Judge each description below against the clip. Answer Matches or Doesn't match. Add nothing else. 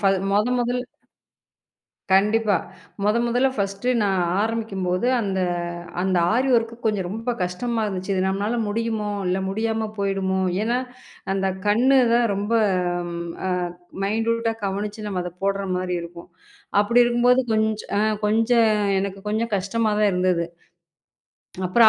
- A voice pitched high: Matches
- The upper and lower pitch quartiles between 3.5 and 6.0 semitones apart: Doesn't match